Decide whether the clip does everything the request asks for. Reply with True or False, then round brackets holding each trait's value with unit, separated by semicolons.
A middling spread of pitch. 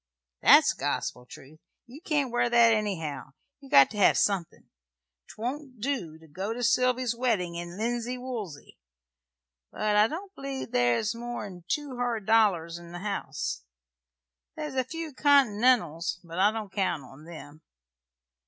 False (6.7 semitones)